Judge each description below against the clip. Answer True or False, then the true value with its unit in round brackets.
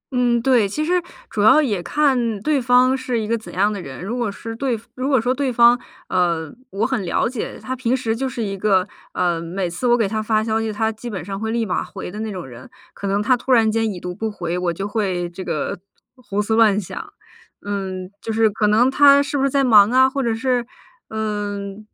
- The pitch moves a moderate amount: True (4.0 semitones)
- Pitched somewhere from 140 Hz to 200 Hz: False (220 Hz)